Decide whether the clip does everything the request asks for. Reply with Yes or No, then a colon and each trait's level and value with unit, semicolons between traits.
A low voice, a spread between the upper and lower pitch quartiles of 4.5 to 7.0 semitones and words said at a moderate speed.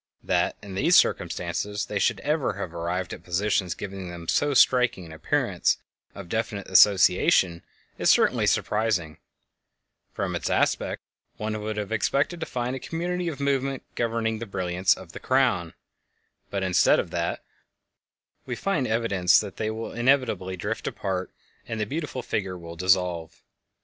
Yes: low, 105 Hz; average, 4.9 semitones; average, 155 wpm